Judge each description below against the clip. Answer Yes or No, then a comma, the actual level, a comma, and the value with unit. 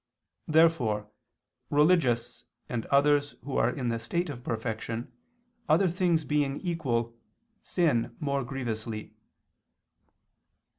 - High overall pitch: No, low, 135 Hz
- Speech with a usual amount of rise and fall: Yes, average, 5.0 semitones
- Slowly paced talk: Yes, slow, 100 wpm